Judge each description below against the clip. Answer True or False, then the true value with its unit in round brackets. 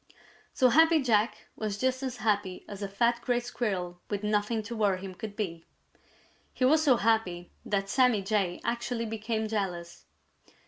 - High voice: True (215 Hz)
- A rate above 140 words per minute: True (165 wpm)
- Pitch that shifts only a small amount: False (3.3 semitones)